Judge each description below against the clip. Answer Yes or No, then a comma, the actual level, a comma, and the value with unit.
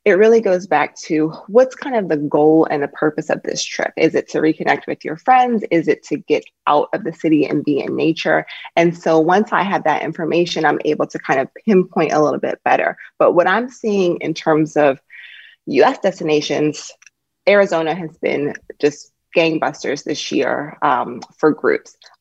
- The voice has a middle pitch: Yes, medium, 165 Hz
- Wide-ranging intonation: No, average, 4.2 semitones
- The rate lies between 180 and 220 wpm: Yes, average, 190 wpm